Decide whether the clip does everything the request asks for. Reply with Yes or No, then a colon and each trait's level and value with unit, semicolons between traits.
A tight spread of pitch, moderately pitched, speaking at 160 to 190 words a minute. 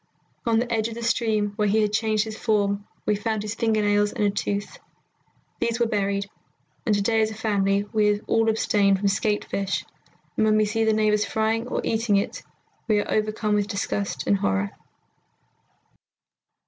No: narrow, 1.4 semitones; high, 210 Hz; average, 185 wpm